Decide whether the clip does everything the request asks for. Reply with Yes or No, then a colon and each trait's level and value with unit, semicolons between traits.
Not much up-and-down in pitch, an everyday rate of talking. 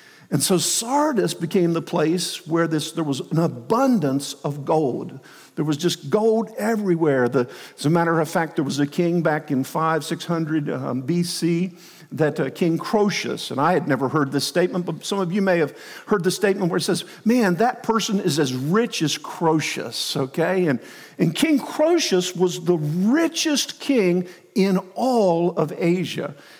No: average, 4.1 semitones; average, 180 wpm